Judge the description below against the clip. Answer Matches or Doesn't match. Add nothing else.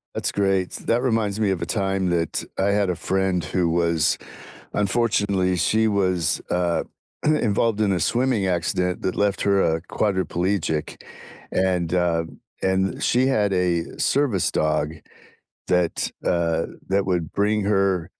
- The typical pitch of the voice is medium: Doesn't match